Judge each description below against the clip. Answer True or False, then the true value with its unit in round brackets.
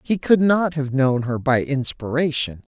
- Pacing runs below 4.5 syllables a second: True (4.3 syllables/s)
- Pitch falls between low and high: True (145 Hz)